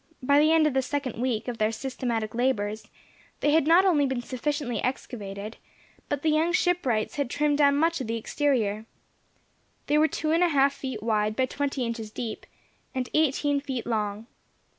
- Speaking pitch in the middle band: No, very high, 265 Hz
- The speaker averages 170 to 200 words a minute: Yes, average, 185 wpm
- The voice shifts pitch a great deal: No, average, 4.6 semitones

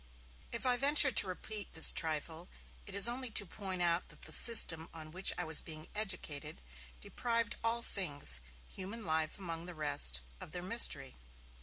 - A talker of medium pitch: Yes, medium, 180 Hz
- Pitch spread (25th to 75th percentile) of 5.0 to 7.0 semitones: Yes, wide, 5.5 semitones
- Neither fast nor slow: Yes, average, 170 wpm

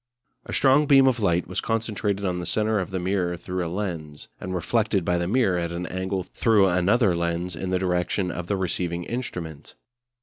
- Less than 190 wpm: No, average, 200 wpm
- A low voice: Yes, very low, 95 Hz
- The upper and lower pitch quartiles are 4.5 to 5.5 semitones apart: No, average, 3.1 semitones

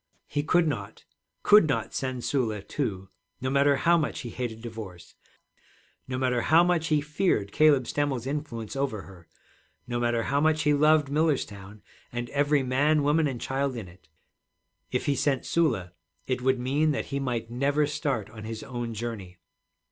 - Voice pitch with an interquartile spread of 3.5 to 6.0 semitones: Yes, average, 4.3 semitones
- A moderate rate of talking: Yes, average, 170 wpm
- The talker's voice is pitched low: Yes, low, 130 Hz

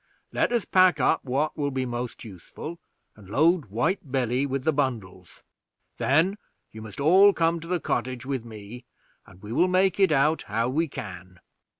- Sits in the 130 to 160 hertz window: Yes, low, 135 Hz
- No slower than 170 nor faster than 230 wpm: Yes, average, 180 wpm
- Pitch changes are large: Yes, wide, 6.4 semitones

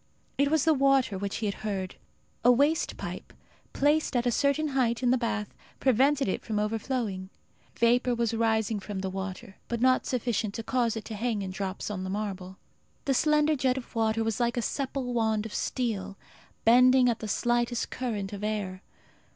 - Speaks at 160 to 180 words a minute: No, average, 190 wpm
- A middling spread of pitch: Yes, average, 3.6 semitones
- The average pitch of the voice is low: No, high, 230 Hz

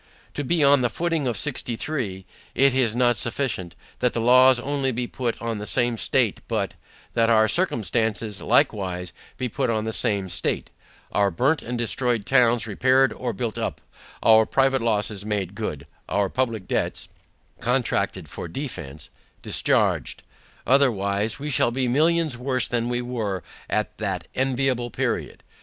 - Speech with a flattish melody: No, average, 3.5 semitones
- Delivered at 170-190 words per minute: No, average, 155 wpm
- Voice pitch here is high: No, low, 120 Hz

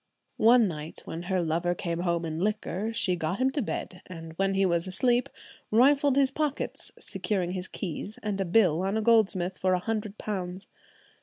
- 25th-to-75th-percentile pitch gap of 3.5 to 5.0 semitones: Yes, average, 4.1 semitones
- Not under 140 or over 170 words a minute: No, average, 185 wpm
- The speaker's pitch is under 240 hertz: Yes, high, 190 Hz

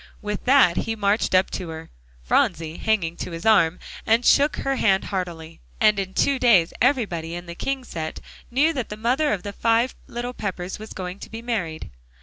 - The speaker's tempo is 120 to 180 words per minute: No, average, 195 wpm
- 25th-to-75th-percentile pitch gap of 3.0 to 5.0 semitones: No, wide, 5.4 semitones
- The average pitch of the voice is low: No, high, 205 Hz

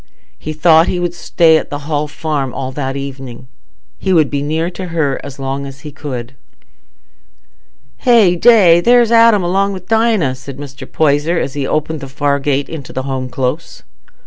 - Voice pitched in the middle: Yes, medium, 150 Hz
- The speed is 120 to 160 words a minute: No, average, 175 wpm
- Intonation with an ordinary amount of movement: Yes, average, 4.1 semitones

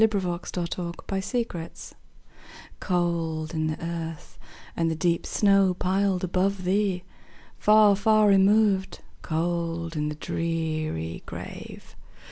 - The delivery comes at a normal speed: No, slow, 105 wpm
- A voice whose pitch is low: No, medium, 175 Hz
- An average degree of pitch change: Yes, average, 3.1 semitones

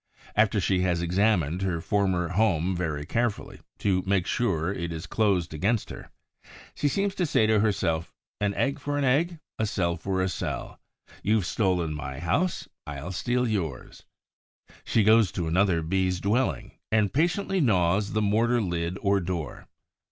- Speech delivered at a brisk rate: No, average, 160 wpm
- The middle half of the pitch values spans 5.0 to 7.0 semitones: No, average, 4.4 semitones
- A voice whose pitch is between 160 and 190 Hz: No, very low, 95 Hz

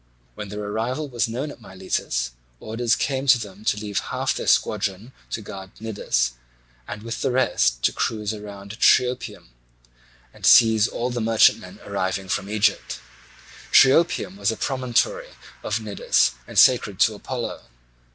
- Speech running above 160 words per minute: No, average, 150 wpm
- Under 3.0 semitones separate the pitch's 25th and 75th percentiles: No, average, 3.7 semitones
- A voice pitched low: Yes, low, 110 Hz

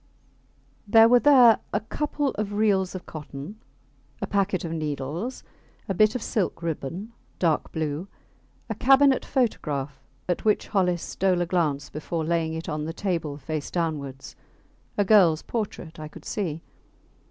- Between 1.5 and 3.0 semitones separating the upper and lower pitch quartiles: No, average, 5.3 semitones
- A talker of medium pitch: Yes, medium, 175 Hz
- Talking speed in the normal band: Yes, average, 150 wpm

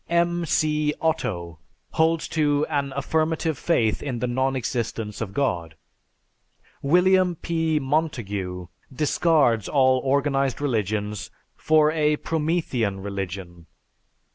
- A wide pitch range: Yes, wide, 6.7 semitones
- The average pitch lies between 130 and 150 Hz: Yes, medium, 140 Hz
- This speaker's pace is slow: Yes, slow, 105 wpm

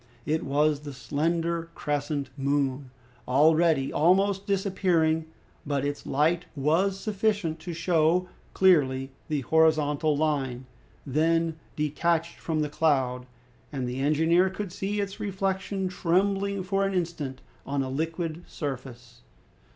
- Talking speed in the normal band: No, slow, 120 wpm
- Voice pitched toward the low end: No, medium, 160 Hz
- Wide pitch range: No, average, 4.1 semitones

